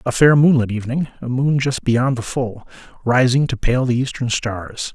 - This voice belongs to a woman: No, male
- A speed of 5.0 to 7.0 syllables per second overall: No, 4.8 syllables/s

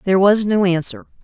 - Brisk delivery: No, average, 195 wpm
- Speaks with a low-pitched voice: No, medium, 185 Hz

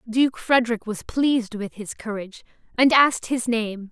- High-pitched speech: Yes, high, 230 Hz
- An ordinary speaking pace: Yes, average, 170 wpm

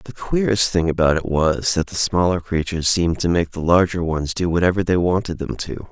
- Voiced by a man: Yes, male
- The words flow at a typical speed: No, fast, 225 wpm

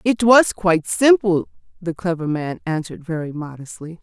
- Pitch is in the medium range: Yes, medium, 180 Hz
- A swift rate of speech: No, average, 150 wpm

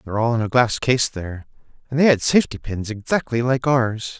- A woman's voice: No, male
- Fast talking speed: Yes, fast, 215 wpm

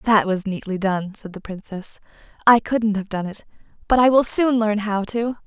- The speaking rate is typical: No, fast, 210 wpm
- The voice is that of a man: No, female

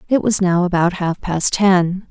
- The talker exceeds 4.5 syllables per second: No, 4.2 syllables/s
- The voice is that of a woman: Yes, female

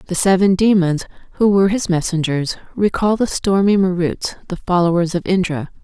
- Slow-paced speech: No, average, 155 wpm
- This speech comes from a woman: Yes, female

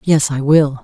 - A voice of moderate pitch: Yes, medium, 145 Hz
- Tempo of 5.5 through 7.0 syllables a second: No, 4.2 syllables/s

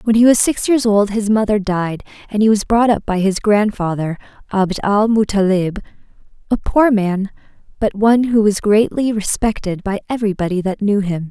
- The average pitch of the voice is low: No, high, 210 Hz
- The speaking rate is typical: Yes, average, 180 wpm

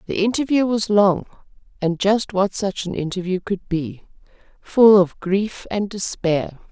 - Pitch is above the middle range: Yes, high, 195 Hz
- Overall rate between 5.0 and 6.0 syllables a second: No, 4.2 syllables/s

